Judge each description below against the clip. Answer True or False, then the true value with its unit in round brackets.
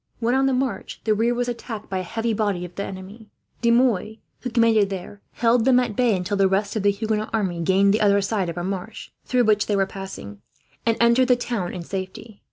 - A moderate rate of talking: False (235 wpm)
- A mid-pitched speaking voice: False (215 Hz)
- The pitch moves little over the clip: False (3.4 semitones)